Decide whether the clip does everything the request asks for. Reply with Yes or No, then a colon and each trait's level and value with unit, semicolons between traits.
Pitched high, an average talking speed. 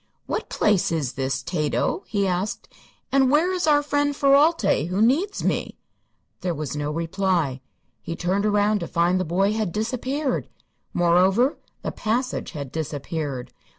Yes: high, 195 Hz; average, 150 wpm